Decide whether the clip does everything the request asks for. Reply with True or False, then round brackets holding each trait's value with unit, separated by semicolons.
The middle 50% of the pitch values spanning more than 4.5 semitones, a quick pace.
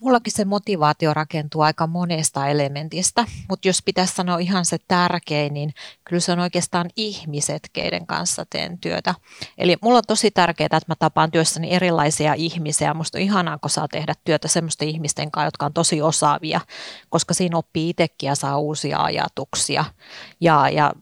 False (2.8 semitones; 170 wpm)